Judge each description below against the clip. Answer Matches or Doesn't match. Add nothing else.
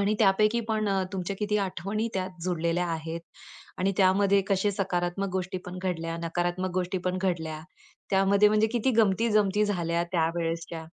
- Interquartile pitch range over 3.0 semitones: Doesn't match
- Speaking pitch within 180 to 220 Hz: Matches